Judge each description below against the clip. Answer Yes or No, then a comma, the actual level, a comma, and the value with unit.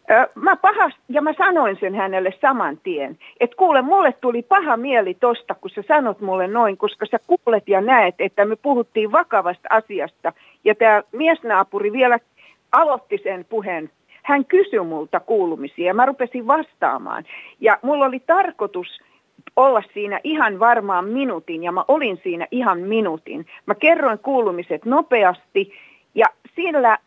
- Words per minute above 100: Yes, average, 150 wpm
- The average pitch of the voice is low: No, high, 240 Hz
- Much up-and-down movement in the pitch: Yes, wide, 7.3 semitones